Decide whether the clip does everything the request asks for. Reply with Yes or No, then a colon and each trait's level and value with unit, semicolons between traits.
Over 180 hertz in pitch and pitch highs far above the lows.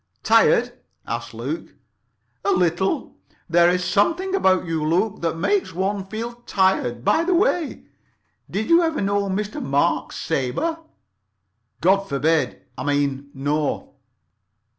Yes: high, 190 Hz; wide, 7.2 semitones